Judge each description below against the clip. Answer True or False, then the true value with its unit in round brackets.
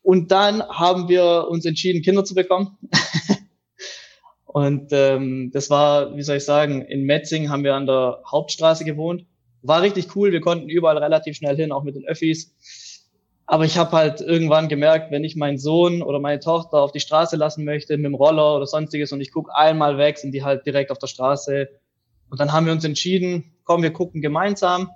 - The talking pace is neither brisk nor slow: False (200 wpm)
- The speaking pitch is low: False (155 Hz)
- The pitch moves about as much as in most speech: True (3.0 semitones)